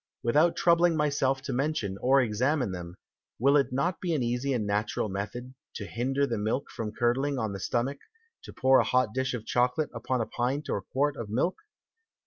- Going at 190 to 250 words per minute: Yes, average, 195 wpm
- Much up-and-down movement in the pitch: No, average, 3.7 semitones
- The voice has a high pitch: No, low, 130 Hz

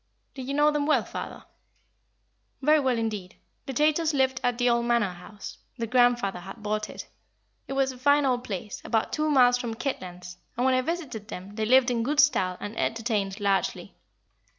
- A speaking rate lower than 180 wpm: No, average, 190 wpm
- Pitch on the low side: No, high, 245 Hz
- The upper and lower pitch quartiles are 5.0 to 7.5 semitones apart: No, average, 4.4 semitones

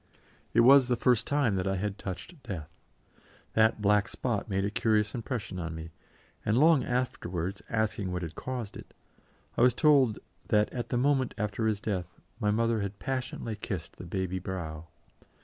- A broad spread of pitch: No, average, 4.4 semitones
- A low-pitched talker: Yes, low, 105 Hz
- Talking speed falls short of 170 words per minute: No, average, 175 wpm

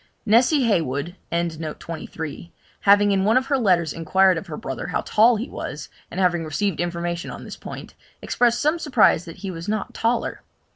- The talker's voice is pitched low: No, high, 190 Hz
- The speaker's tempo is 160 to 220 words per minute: Yes, average, 175 wpm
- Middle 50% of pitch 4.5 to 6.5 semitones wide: Yes, average, 5.1 semitones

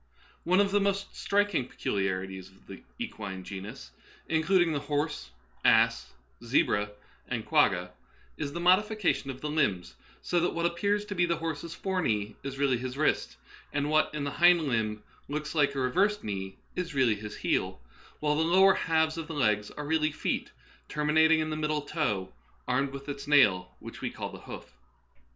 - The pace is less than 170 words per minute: No, average, 185 wpm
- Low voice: No, medium, 150 Hz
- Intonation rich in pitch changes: Yes, wide, 6.2 semitones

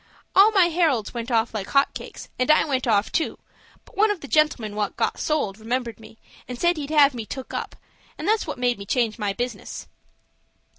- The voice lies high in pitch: Yes, very high, 255 Hz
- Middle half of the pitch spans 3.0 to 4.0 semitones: No, wide, 5.5 semitones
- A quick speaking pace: Yes, fast, 210 wpm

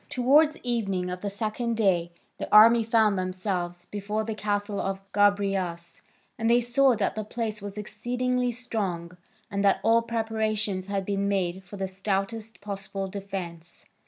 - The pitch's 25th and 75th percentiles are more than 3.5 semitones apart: No, average, 2.8 semitones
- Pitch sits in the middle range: No, high, 205 Hz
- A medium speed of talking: Yes, average, 155 wpm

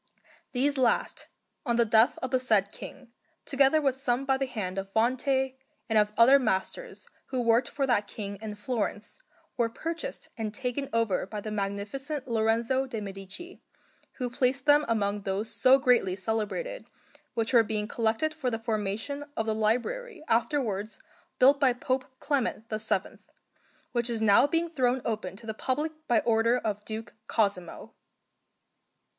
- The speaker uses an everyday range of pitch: Yes, average, 3.7 semitones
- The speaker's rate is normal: Yes, average, 160 wpm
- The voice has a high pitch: Yes, high, 235 Hz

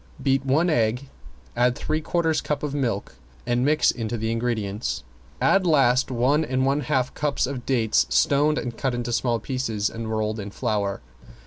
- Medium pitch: No, low, 125 Hz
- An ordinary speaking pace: Yes, average, 175 wpm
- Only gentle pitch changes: No, average, 3.7 semitones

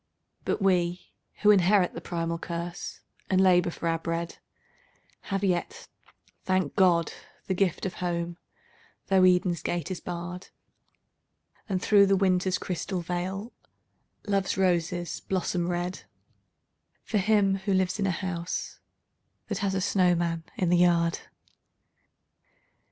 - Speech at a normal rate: No, slow, 130 wpm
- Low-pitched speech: No, medium, 180 Hz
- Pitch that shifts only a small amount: Yes, narrow, 1.8 semitones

